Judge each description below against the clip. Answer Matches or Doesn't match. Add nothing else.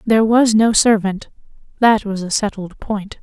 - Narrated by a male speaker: Doesn't match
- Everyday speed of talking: Matches